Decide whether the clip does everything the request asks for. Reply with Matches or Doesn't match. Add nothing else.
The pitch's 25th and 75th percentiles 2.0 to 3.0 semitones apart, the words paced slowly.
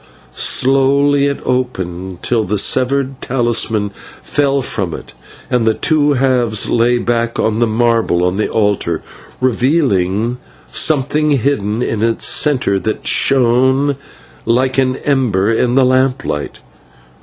Doesn't match